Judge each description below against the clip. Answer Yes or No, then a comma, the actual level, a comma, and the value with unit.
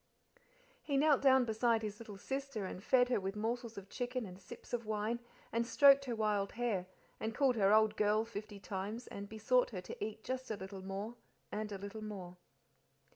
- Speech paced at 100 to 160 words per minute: No, average, 195 wpm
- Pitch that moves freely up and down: No, average, 3.2 semitones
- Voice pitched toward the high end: Yes, high, 220 Hz